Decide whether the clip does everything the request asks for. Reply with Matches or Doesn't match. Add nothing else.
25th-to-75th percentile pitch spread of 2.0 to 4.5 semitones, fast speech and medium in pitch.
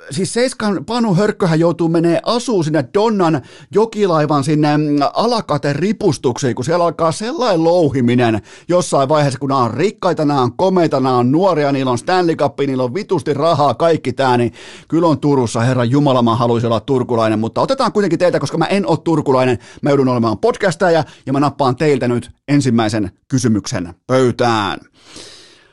Doesn't match